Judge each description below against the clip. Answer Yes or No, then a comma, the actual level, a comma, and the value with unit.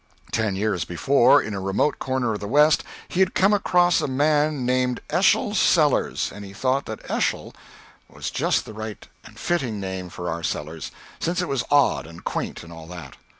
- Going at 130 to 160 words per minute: No, average, 195 wpm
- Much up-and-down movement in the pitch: Yes, wide, 7.5 semitones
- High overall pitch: No, low, 115 Hz